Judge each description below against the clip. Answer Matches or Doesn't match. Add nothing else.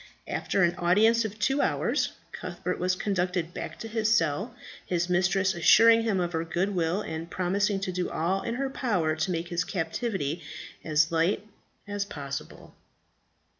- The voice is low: Doesn't match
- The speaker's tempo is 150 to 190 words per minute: Matches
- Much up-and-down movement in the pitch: Doesn't match